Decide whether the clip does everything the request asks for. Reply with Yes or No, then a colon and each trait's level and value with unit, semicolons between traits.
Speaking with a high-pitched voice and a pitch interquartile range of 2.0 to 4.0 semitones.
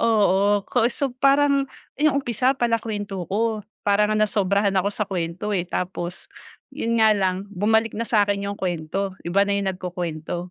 Yes: high, 205 Hz; average, 3.1 semitones